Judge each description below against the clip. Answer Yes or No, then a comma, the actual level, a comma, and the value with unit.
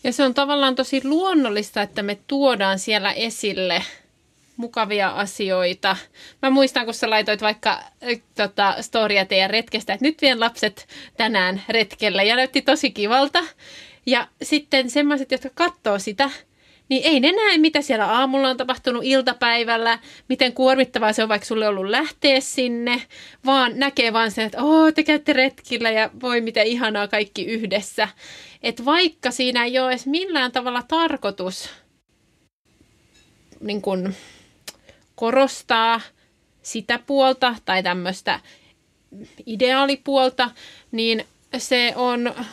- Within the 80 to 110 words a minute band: No, average, 130 wpm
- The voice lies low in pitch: No, high, 245 Hz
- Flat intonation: No, average, 3.9 semitones